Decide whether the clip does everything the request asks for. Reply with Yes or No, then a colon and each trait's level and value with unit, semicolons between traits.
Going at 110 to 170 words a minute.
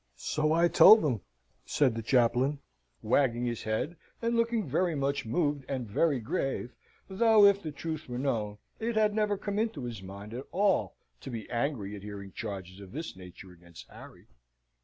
No: average, 180 wpm